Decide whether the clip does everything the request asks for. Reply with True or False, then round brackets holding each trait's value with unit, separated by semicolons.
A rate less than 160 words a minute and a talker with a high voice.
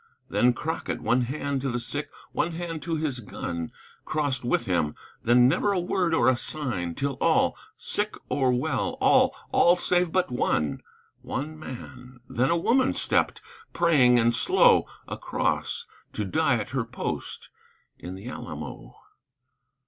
False (150 wpm; 130 Hz)